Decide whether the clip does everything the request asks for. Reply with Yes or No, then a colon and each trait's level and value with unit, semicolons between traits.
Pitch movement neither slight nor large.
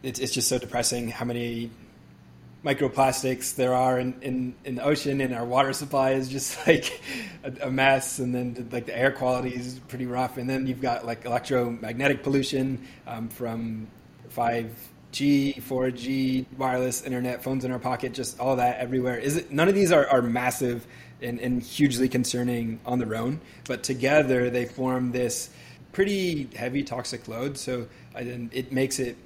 No: narrow, 1.5 semitones